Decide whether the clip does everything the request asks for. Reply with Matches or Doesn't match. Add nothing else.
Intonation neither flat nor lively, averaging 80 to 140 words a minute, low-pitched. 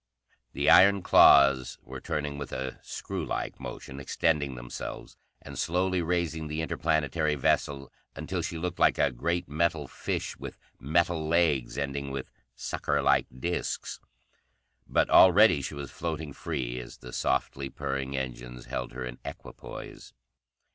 Matches